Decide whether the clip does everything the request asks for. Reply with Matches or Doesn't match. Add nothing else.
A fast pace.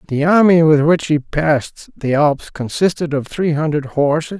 Doesn't match